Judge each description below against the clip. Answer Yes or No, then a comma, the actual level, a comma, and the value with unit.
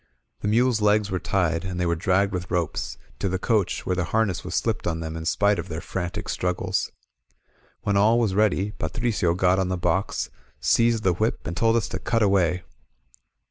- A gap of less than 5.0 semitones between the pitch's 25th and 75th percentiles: Yes, average, 3.2 semitones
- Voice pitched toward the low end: Yes, very low, 95 Hz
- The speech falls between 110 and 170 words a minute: No, average, 200 wpm